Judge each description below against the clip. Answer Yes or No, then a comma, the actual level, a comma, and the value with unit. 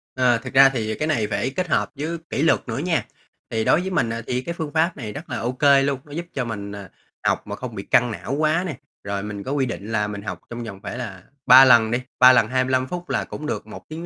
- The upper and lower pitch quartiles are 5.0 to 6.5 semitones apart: Yes, wide, 5.4 semitones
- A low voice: Yes, low, 130 Hz